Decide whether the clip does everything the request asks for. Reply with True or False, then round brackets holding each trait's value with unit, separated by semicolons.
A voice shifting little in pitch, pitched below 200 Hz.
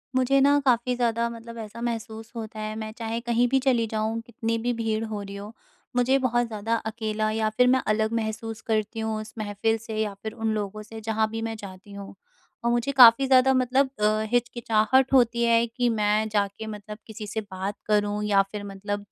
False (1.9 semitones; 225 Hz)